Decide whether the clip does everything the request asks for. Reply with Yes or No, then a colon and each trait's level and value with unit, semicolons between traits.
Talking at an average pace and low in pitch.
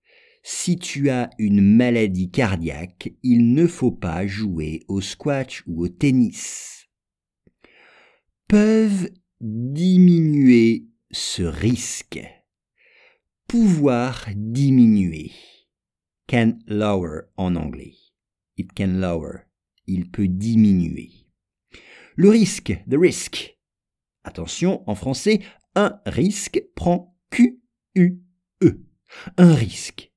No: slow, 95 wpm; low, 125 Hz